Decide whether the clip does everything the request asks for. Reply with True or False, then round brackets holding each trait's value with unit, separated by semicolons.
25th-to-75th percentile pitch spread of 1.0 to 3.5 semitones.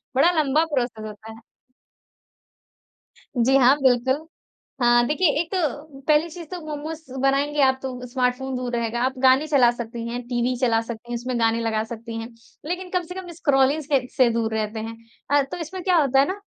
False (4.1 semitones)